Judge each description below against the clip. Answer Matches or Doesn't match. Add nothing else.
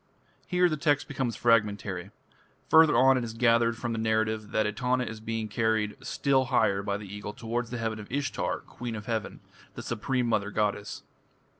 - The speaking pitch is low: Matches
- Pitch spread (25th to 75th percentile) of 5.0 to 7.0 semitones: Doesn't match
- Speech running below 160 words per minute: Doesn't match